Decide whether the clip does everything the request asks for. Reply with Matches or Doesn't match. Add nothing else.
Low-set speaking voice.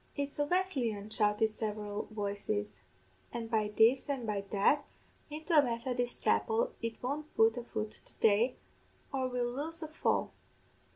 Doesn't match